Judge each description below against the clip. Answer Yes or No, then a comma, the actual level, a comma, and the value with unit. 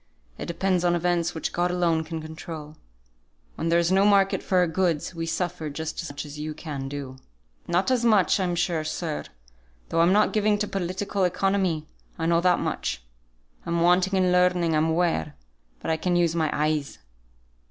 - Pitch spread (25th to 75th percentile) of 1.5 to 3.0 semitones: Yes, narrow, 2.4 semitones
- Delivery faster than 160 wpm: Yes, average, 185 wpm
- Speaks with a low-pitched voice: No, medium, 170 Hz